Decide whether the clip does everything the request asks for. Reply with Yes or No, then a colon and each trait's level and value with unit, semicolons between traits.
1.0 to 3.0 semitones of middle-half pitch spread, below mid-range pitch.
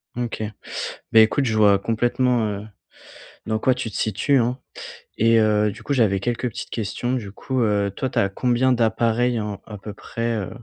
Yes: narrow, 2.6 semitones; low, 115 Hz